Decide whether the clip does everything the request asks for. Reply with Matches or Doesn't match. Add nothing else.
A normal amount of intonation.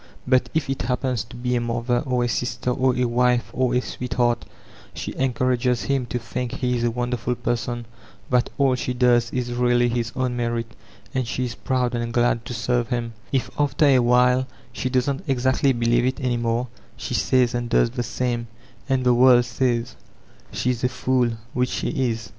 Doesn't match